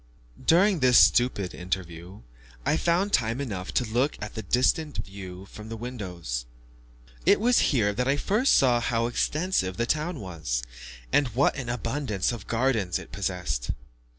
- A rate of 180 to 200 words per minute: No, average, 155 wpm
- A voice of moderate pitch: No, low, 115 Hz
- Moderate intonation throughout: No, wide, 6.6 semitones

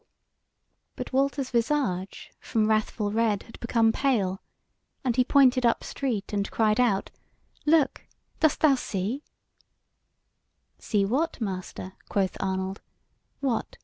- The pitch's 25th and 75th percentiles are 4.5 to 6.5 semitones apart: Yes, average, 5.0 semitones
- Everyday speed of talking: No, slow, 115 wpm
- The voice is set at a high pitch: Yes, high, 225 Hz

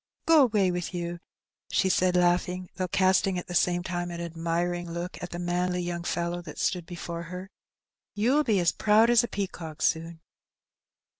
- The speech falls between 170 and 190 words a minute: Yes, average, 180 wpm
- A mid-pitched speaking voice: Yes, medium, 175 Hz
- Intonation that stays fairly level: Yes, narrow, 1.6 semitones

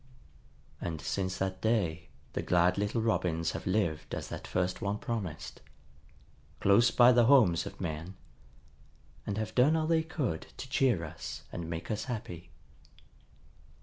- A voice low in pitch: Yes, very low, 95 Hz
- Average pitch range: No, wide, 5.7 semitones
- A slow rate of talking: No, average, 150 wpm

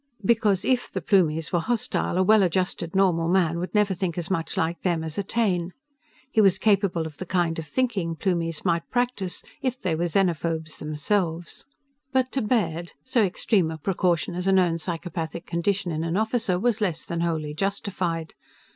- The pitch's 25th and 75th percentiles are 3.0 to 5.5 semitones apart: Yes, average, 3.3 semitones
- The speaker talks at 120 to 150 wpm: No, average, 180 wpm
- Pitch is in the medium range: Yes, medium, 180 Hz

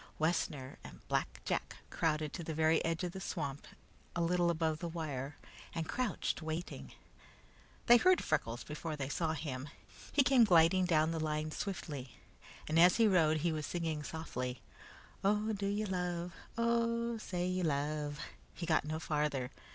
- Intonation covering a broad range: No, average, 3.2 semitones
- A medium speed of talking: Yes, average, 165 wpm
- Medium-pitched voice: Yes, medium, 165 Hz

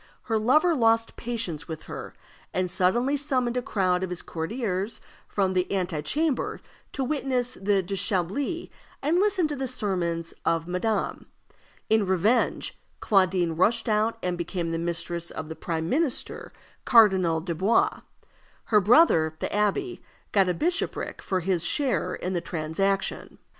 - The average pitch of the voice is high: Yes, high, 195 Hz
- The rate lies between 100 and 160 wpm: Yes, average, 145 wpm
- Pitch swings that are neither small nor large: No, wide, 5.8 semitones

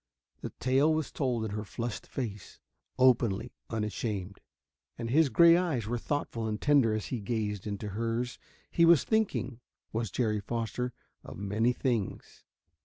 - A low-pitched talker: Yes, low, 115 Hz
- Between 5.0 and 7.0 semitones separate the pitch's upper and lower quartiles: No, average, 3.4 semitones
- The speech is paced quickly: No, average, 150 wpm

